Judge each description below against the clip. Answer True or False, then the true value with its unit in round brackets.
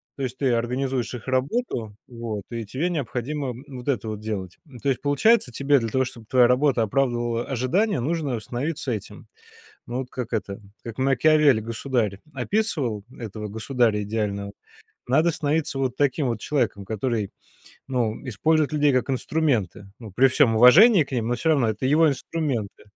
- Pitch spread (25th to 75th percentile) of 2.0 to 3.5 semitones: False (4.1 semitones)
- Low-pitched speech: True (125 Hz)